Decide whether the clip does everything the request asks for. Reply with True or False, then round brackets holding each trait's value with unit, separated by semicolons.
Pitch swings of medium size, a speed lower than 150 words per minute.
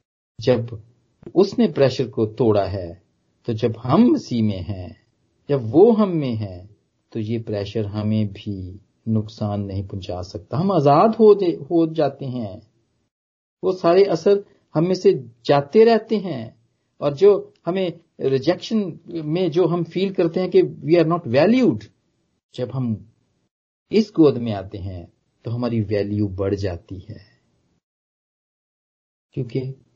False (8.3 semitones; 135 wpm)